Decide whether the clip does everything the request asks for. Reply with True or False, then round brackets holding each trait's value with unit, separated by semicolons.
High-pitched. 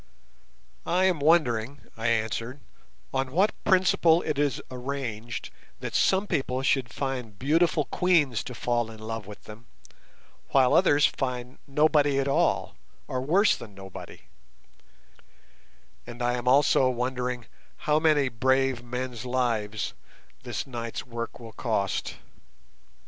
False (130 Hz)